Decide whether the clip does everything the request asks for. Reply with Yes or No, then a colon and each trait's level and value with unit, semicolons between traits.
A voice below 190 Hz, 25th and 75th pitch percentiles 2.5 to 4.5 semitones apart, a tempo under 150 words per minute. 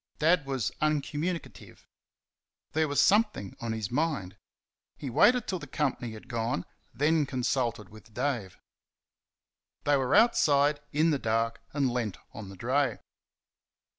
No: low, 135 Hz; average, 4.9 semitones; slow, 135 wpm